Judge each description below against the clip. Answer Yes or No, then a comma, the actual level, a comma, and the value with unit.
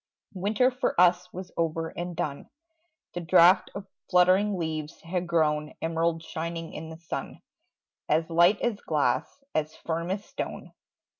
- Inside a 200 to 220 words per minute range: No, average, 145 wpm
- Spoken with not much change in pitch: Yes, narrow, 2.2 semitones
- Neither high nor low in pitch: Yes, medium, 170 Hz